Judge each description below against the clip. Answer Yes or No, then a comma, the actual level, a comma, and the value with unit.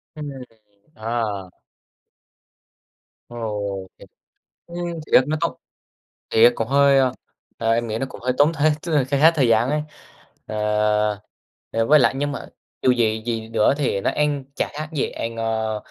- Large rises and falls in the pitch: No, average, 4.4 semitones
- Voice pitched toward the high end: No, low, 120 Hz